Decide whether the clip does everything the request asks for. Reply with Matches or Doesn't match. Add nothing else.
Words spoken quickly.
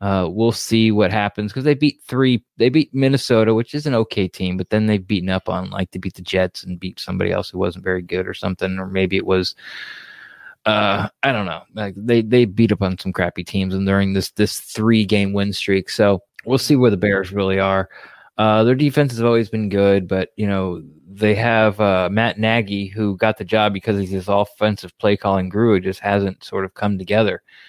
Matches